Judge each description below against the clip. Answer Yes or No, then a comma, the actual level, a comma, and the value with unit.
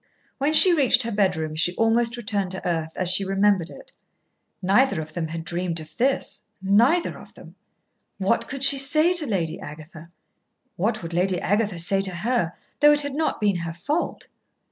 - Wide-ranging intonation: Yes, wide, 6.9 semitones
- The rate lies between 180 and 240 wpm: Yes, average, 185 wpm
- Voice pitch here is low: No, high, 195 Hz